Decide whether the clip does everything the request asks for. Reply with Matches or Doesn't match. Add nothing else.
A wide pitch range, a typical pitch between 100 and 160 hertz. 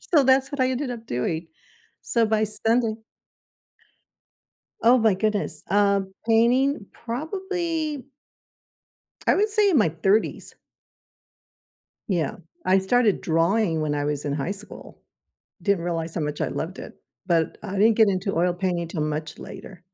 Doesn't match